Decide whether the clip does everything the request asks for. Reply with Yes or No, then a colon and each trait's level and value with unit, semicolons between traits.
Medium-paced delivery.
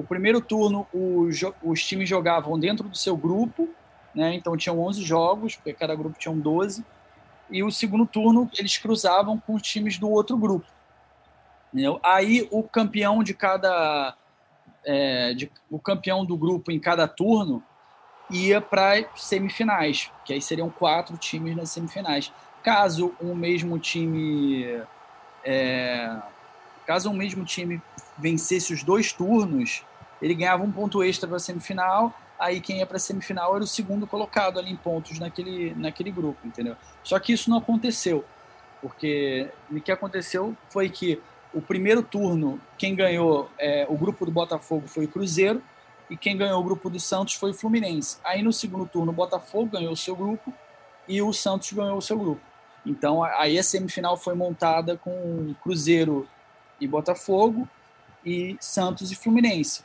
Yes: average, 160 wpm